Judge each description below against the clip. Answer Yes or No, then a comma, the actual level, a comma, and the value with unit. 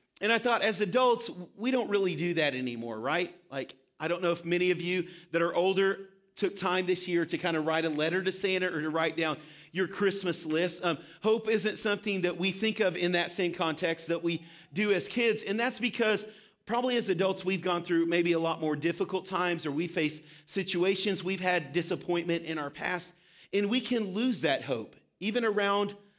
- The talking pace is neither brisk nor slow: No, fast, 210 wpm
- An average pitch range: Yes, average, 3.2 semitones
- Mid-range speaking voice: Yes, medium, 180 Hz